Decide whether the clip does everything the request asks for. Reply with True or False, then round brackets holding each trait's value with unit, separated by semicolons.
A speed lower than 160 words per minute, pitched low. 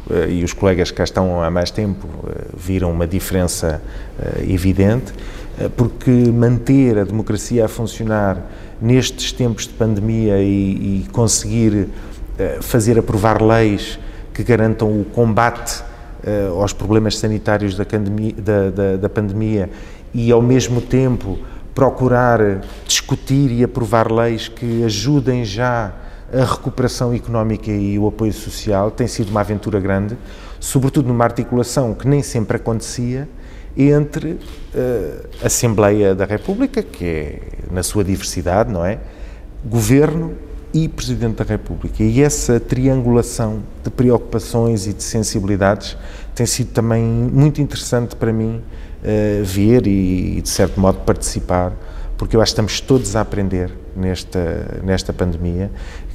True (140 wpm; 110 Hz)